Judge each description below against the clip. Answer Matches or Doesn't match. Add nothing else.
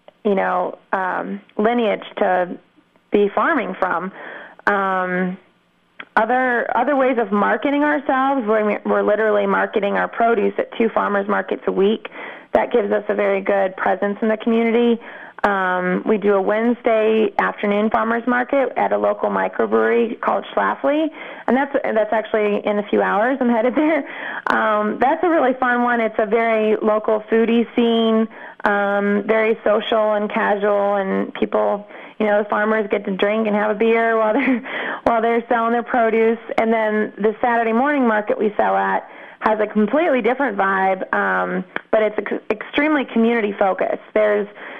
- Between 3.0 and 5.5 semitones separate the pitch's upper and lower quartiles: Doesn't match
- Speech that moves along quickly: Doesn't match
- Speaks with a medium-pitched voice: Doesn't match